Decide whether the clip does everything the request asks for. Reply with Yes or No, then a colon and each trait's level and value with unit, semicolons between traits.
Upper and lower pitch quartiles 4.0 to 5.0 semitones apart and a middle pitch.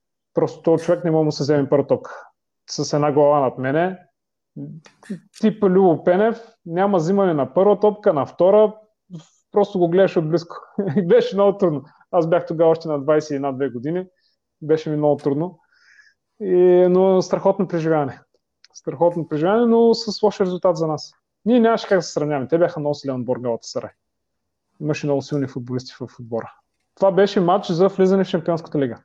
Yes: average, 4.7 semitones; medium, 175 Hz